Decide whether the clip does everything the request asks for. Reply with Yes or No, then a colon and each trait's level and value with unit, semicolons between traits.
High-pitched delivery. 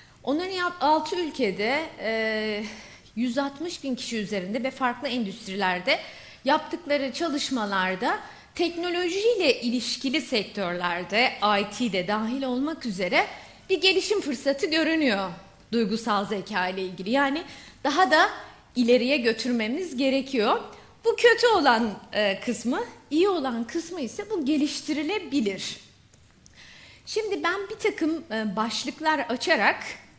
Yes: very high, 270 Hz